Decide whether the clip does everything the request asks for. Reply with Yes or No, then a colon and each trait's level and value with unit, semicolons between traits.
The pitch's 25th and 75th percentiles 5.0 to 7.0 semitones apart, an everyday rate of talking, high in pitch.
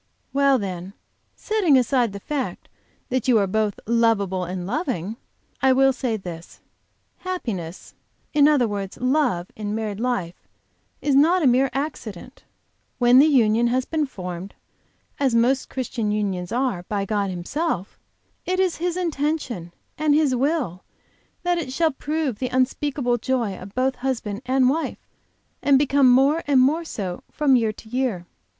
Yes: wide, 5.5 semitones; average, 155 wpm; very high, 250 Hz